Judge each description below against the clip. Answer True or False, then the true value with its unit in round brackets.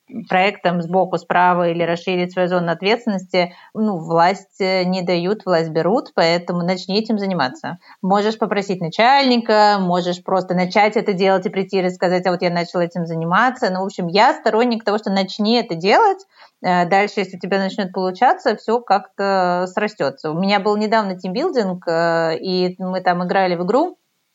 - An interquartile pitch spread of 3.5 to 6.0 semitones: False (2.8 semitones)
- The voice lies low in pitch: False (190 Hz)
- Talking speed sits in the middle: False (165 wpm)